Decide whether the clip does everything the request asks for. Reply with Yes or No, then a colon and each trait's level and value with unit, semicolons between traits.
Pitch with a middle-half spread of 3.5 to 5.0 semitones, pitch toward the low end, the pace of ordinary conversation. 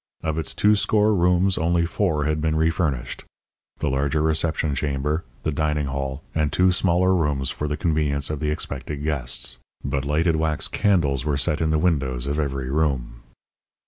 No: average, 2.9 semitones; very low, 75 Hz; average, 175 wpm